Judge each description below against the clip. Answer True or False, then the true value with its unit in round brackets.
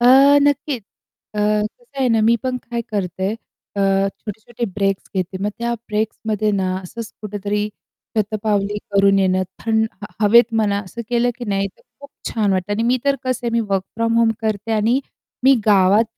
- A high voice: True (215 Hz)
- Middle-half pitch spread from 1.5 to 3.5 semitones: True (2.8 semitones)